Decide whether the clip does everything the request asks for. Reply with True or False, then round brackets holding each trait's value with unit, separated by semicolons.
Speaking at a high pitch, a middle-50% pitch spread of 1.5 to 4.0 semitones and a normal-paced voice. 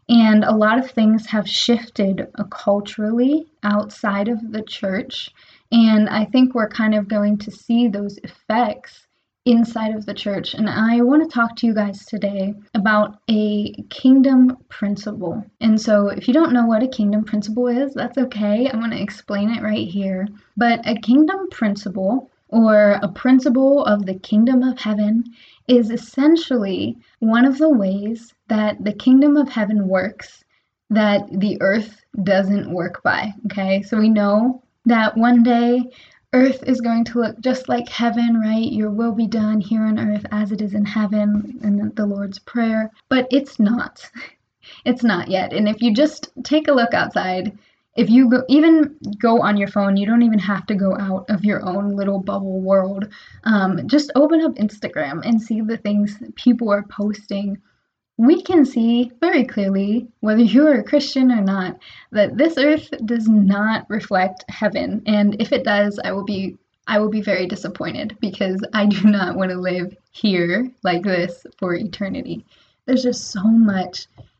True (215 Hz; 2.9 semitones; 175 wpm)